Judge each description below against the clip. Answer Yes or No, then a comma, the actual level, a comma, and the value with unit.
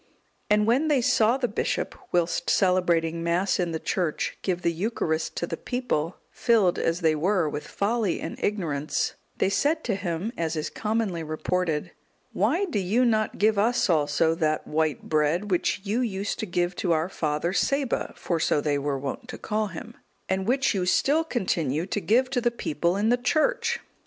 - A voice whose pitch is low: No, medium, 185 Hz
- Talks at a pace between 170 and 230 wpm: Yes, average, 185 wpm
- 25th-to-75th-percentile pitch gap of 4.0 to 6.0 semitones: Yes, wide, 5.6 semitones